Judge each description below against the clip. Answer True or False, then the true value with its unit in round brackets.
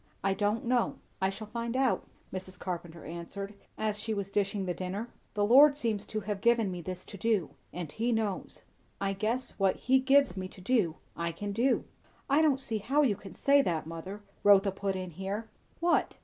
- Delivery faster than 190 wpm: True (200 wpm)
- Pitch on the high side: True (205 Hz)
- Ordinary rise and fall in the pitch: True (3.8 semitones)